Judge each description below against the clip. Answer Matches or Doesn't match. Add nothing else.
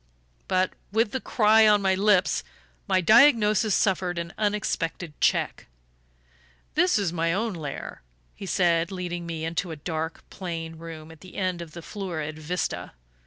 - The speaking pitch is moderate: Matches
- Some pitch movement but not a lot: Matches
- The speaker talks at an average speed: Matches